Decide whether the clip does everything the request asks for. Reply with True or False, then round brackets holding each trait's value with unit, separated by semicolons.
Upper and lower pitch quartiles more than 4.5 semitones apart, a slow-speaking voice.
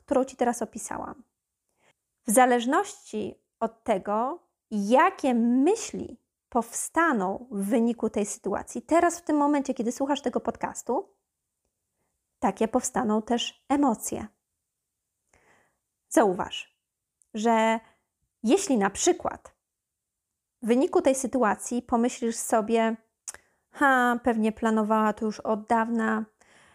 False (3.4 semitones; 100 wpm)